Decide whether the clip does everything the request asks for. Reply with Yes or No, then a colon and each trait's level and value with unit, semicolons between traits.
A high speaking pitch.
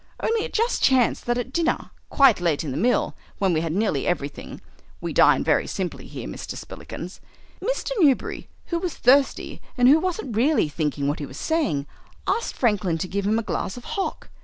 Yes: high, 235 Hz